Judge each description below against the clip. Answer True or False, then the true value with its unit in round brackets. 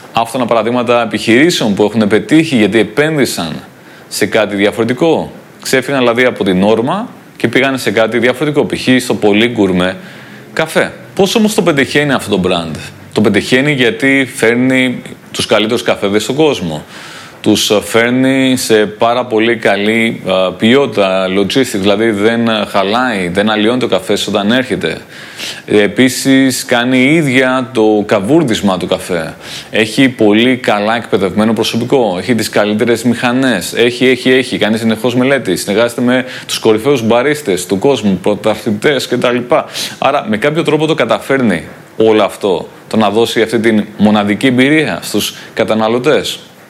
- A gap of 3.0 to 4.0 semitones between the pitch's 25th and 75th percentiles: True (3.6 semitones)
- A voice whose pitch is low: True (115 Hz)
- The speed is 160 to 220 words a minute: False (140 wpm)